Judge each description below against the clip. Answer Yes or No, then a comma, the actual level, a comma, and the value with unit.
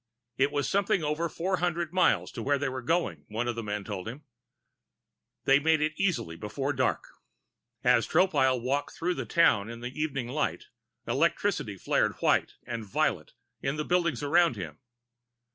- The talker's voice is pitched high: No, medium, 140 Hz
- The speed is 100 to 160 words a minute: No, average, 170 wpm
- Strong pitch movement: Yes, wide, 5.8 semitones